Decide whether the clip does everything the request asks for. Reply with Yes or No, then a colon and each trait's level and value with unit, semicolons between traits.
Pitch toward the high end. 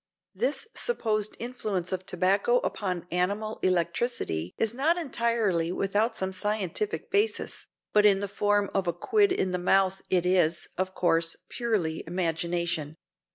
Yes: high, 195 Hz